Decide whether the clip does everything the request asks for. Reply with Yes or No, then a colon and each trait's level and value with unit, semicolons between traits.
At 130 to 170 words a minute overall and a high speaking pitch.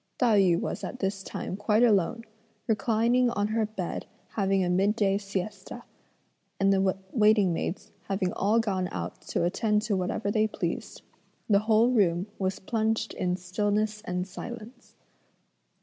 Yes: average, 150 wpm; high, 205 Hz